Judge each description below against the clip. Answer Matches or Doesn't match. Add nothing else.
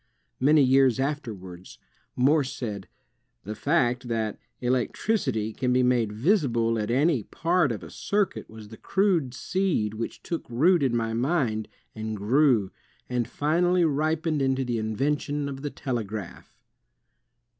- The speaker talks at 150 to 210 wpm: Doesn't match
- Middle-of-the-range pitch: Doesn't match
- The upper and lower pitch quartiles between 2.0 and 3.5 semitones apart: Doesn't match